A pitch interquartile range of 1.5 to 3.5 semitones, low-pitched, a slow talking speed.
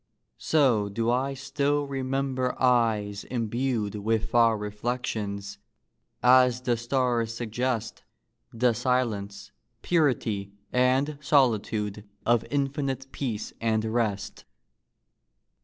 Yes: average, 3.2 semitones; low, 120 Hz; slow, 90 wpm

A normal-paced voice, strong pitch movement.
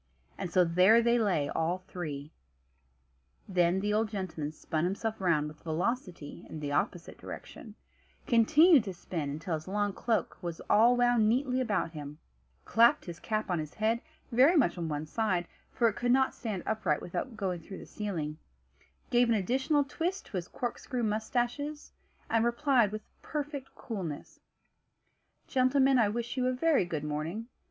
Yes: average, 165 wpm; wide, 6.1 semitones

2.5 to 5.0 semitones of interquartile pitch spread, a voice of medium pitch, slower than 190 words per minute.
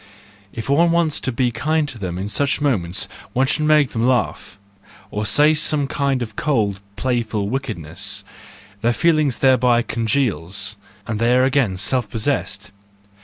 No: average, 4.7 semitones; low, 125 Hz; average, 155 wpm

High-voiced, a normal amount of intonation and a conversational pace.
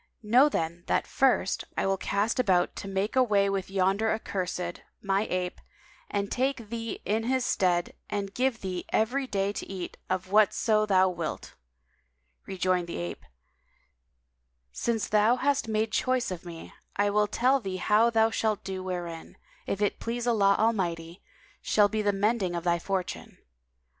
Yes: high, 200 Hz; average, 3.3 semitones; average, 160 wpm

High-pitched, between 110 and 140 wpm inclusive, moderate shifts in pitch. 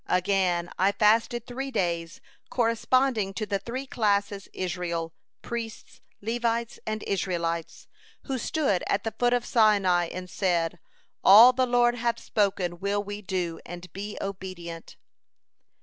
Yes: high, 200 Hz; slow, 135 wpm; average, 4.6 semitones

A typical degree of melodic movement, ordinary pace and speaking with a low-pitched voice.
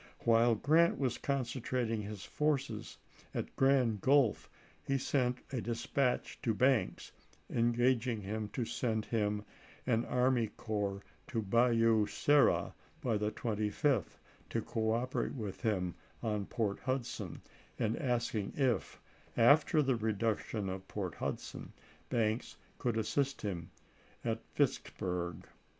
No: average, 3.3 semitones; slow, 125 wpm; low, 115 Hz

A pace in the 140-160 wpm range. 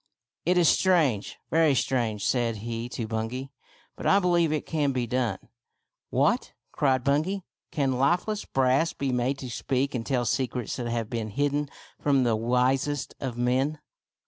No: average, 180 wpm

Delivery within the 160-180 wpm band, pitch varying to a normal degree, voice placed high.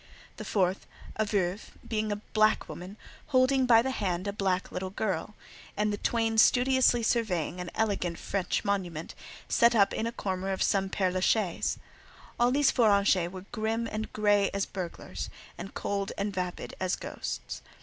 Yes: average, 170 wpm; average, 3.1 semitones; high, 205 Hz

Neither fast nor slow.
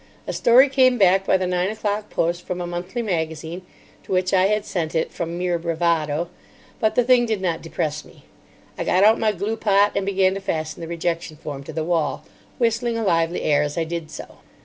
No: fast, 215 wpm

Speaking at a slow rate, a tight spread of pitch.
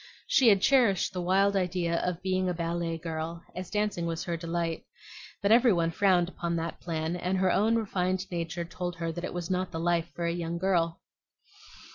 No: average, 200 wpm; narrow, 2.0 semitones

